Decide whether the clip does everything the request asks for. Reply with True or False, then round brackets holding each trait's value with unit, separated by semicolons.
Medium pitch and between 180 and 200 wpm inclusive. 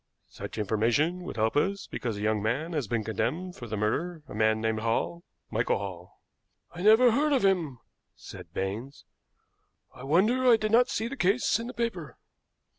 True (150 Hz; 185 wpm)